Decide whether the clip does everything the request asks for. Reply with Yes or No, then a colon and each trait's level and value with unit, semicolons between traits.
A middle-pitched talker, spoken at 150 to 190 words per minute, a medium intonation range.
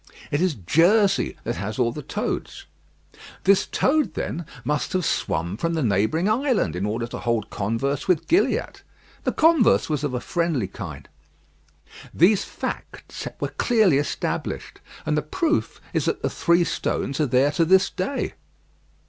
No: medium, 150 Hz; average, 155 wpm; wide, 8.1 semitones